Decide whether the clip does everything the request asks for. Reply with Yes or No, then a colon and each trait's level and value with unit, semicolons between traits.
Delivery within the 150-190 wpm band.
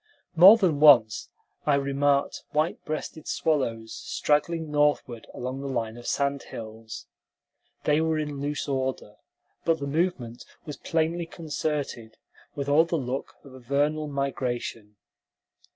No: slow, 135 wpm